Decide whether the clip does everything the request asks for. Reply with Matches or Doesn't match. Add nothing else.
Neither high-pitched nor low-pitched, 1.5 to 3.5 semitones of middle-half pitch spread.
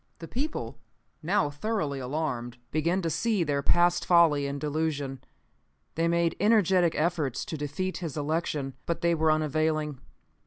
Matches